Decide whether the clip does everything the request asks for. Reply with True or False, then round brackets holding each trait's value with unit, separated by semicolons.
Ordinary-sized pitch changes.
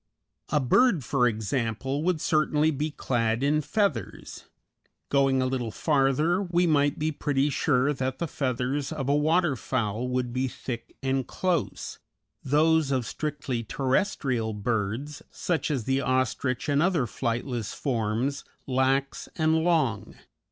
True (3.5 semitones)